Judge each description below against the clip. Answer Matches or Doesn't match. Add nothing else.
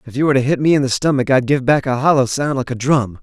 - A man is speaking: Matches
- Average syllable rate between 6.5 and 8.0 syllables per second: Matches